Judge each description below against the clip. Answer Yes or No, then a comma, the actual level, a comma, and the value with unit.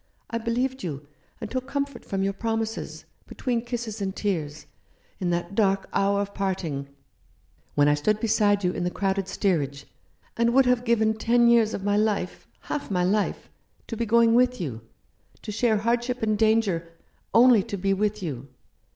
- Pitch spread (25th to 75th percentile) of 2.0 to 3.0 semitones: No, average, 3.7 semitones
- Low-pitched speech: No, high, 210 Hz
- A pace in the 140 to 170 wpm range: No, average, 185 wpm